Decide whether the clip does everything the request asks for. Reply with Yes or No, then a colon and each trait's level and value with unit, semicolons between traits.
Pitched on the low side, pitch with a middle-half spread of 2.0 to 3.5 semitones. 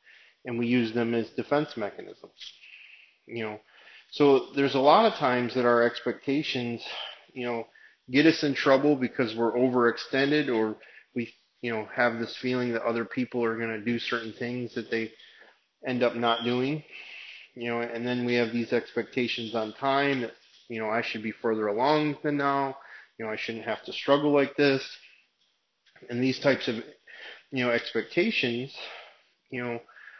Yes: low, 120 Hz; average, 2.8 semitones